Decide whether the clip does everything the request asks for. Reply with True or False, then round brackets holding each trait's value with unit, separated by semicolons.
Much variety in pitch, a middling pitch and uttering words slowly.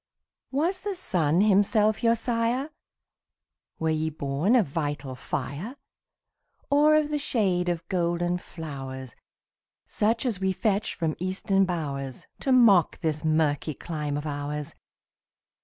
True (7.2 semitones; 175 Hz; 125 wpm)